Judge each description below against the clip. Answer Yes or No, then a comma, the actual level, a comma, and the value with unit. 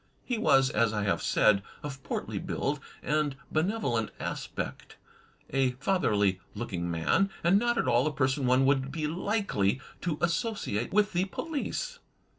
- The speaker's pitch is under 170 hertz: Yes, medium, 140 Hz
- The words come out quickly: No, average, 150 wpm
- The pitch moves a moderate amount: No, wide, 8.6 semitones